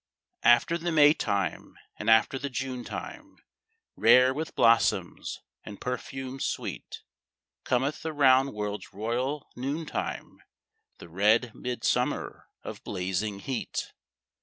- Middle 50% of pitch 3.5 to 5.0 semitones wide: Yes, average, 4.1 semitones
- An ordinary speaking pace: No, slow, 115 wpm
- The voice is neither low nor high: No, low, 125 Hz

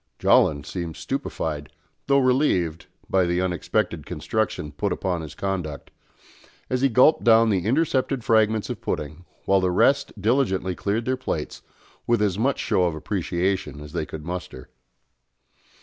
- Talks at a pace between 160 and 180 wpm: No, average, 150 wpm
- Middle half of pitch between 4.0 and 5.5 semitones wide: Yes, average, 5.2 semitones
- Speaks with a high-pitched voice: No, very low, 95 Hz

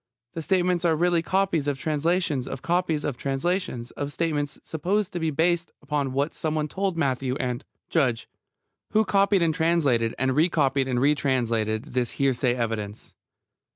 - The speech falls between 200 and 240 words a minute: No, average, 160 wpm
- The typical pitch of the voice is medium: Yes, medium, 150 Hz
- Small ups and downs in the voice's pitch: No, average, 4.7 semitones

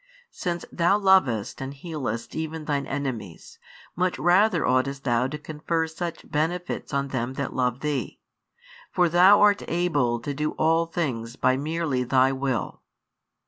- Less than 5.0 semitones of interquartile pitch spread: Yes, average, 4.6 semitones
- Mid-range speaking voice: Yes, medium, 150 Hz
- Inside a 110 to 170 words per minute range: Yes, average, 145 wpm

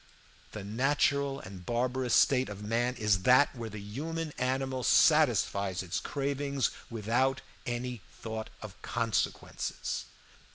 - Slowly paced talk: Yes, slow, 120 wpm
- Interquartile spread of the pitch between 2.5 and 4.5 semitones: Yes, average, 4.0 semitones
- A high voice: No, low, 120 Hz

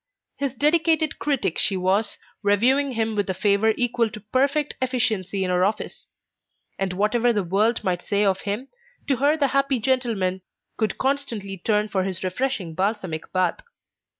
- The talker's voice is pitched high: Yes, high, 215 Hz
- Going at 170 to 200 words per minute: No, average, 160 wpm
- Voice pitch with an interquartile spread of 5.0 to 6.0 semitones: Yes, average, 5.3 semitones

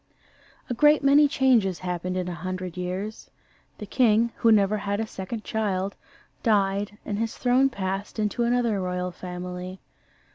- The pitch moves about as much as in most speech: Yes, average, 3.8 semitones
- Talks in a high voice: Yes, high, 200 Hz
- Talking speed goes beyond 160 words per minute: No, average, 150 wpm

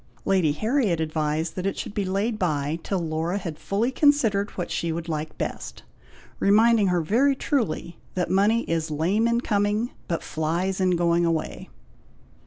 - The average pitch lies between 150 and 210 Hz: Yes, medium, 185 Hz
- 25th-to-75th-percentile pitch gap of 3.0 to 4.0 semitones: No, average, 4.6 semitones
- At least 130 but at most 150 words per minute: No, average, 165 wpm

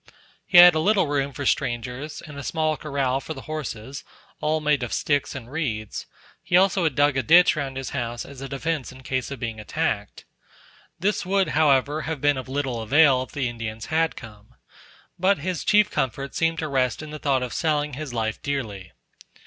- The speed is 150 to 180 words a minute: No, average, 200 wpm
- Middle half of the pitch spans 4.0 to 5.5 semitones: No, average, 3.6 semitones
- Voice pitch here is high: No, medium, 140 Hz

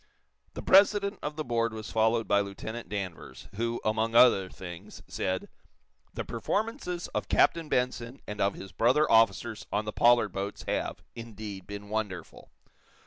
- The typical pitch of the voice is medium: No, low, 110 Hz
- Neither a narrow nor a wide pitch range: Yes, average, 3.1 semitones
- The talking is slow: No, average, 150 wpm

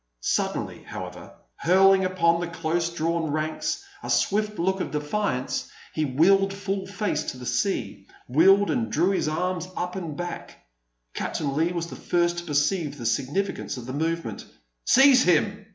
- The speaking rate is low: No, average, 160 wpm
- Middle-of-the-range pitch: Yes, medium, 175 Hz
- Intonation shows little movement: No, average, 4.0 semitones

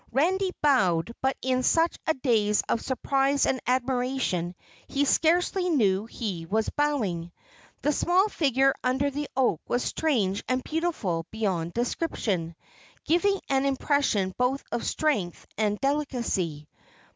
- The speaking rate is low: Yes, slow, 130 wpm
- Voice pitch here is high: Yes, very high, 255 Hz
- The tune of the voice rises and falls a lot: Yes, wide, 6.0 semitones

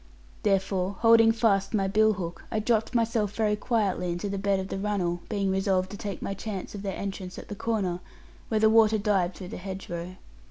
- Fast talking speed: Yes, fast, 210 wpm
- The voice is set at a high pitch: Yes, high, 200 Hz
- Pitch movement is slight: Yes, narrow, 2.3 semitones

